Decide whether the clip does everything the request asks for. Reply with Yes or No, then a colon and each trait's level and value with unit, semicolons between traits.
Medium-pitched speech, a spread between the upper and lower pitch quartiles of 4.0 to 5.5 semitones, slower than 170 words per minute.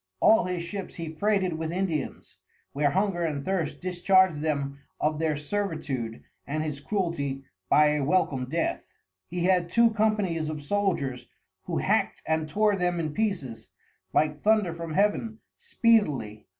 Yes: medium, 165 Hz; average, 4.5 semitones; average, 150 wpm